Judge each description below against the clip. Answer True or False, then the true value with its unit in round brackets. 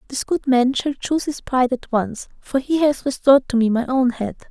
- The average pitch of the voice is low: False (260 Hz)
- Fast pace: True (240 wpm)